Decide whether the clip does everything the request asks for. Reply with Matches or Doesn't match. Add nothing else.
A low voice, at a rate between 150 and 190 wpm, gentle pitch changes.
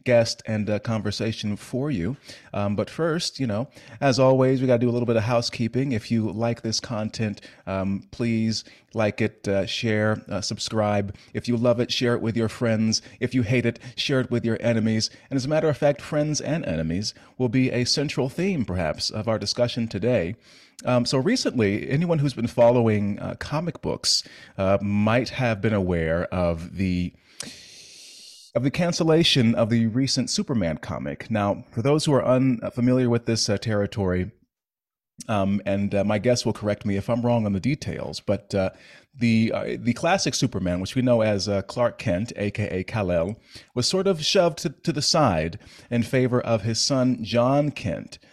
Doesn't match